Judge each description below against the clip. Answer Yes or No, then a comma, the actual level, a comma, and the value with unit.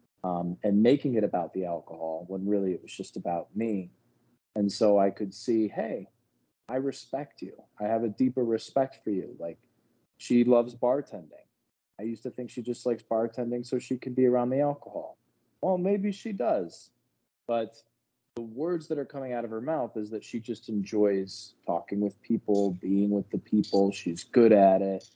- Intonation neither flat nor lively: Yes, average, 3.6 semitones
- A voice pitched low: Yes, low, 115 Hz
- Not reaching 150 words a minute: No, average, 190 wpm